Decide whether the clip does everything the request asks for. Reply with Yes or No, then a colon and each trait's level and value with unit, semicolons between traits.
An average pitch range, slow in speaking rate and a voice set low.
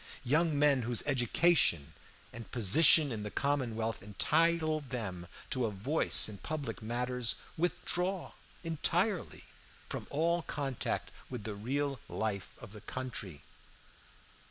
No: wide, 6.1 semitones; slow, 120 wpm; low, 130 Hz